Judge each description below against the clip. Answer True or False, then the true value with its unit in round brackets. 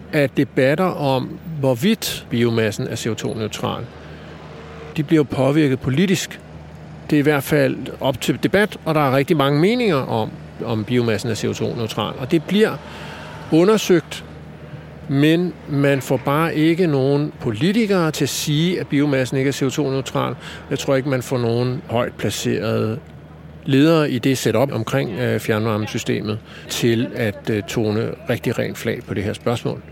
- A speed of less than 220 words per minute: True (145 wpm)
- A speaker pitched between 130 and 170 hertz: True (135 Hz)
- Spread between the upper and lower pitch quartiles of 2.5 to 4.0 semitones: False (4.8 semitones)